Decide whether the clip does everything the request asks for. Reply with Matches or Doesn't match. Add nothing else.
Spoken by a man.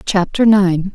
Doesn't match